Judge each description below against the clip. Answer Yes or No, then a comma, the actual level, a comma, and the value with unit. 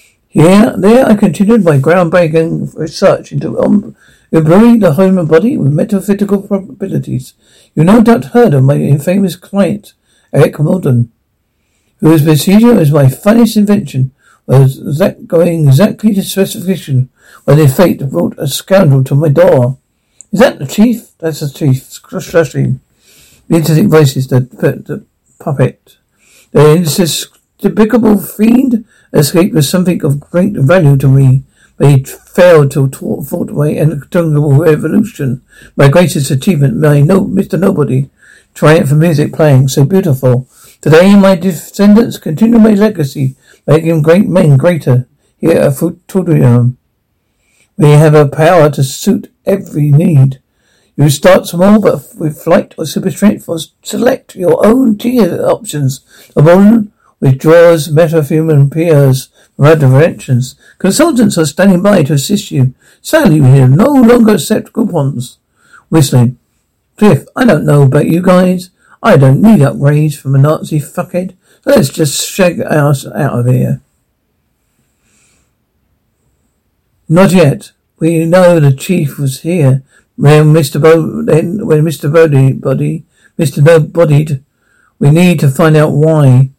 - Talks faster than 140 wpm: No, slow, 135 wpm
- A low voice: No, medium, 160 Hz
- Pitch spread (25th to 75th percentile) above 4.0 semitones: Yes, average, 5.3 semitones